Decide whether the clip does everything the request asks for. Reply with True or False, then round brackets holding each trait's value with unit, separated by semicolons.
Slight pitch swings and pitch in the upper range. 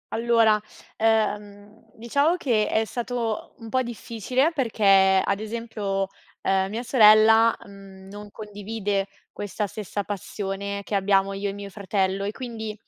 True (2.3 semitones; 210 Hz)